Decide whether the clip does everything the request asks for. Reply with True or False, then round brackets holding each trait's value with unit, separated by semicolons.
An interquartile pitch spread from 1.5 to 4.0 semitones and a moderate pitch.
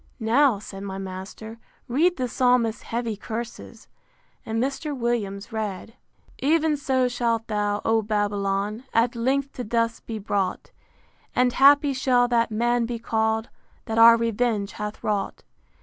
False (2.8 semitones; 230 Hz)